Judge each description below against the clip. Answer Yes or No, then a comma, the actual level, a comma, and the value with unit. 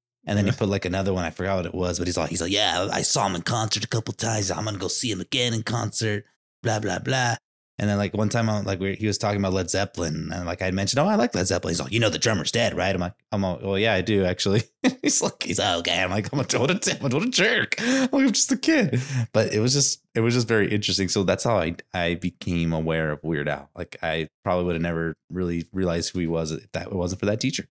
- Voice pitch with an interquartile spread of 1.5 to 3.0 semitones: No, average, 4.2 semitones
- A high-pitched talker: No, low, 100 Hz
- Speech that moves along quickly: Yes, fast, 285 wpm